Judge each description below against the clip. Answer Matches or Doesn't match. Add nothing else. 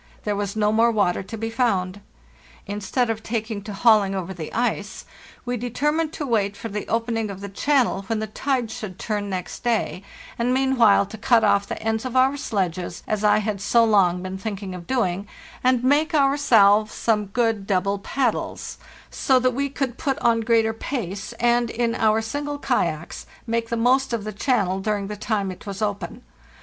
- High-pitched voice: Matches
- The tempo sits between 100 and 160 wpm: Doesn't match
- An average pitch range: Matches